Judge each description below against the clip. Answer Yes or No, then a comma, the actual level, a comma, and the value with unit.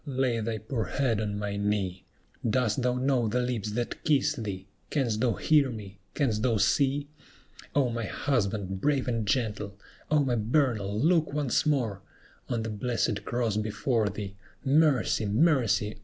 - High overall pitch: No, low, 115 Hz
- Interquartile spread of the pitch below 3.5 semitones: No, average, 4.2 semitones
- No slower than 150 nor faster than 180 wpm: Yes, average, 155 wpm